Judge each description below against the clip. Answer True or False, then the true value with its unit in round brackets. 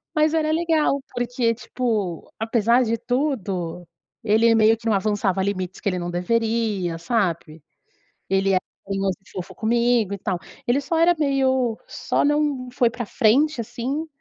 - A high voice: True (230 Hz)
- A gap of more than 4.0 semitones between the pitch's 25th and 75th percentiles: True (4.7 semitones)